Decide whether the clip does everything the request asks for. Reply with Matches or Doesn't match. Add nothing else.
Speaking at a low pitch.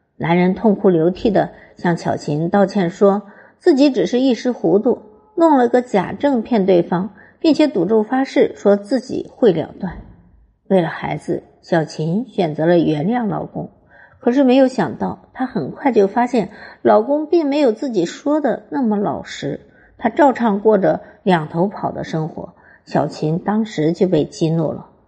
Doesn't match